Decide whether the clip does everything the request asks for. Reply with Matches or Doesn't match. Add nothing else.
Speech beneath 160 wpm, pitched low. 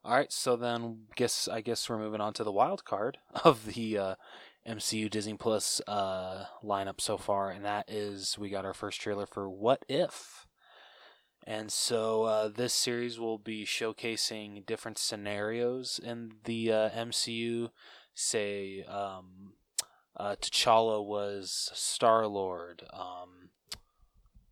Matches